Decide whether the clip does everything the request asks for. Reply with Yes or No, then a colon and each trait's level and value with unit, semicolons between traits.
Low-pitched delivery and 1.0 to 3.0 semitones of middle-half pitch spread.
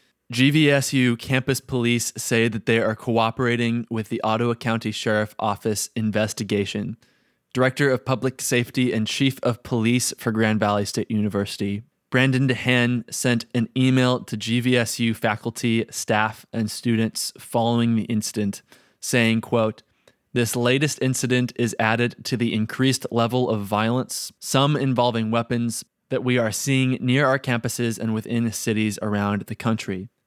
Yes: low, 115 Hz; narrow, 2.4 semitones